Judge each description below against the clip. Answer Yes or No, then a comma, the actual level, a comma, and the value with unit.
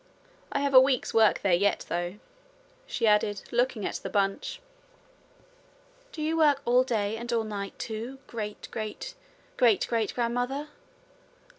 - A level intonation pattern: No, average, 3.7 semitones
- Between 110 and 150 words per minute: Yes, average, 145 wpm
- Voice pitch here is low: No, high, 230 Hz